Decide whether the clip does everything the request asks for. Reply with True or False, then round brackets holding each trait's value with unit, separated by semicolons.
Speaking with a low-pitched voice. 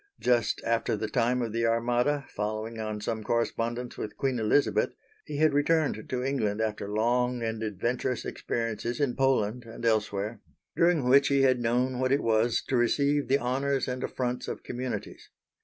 True (120 Hz)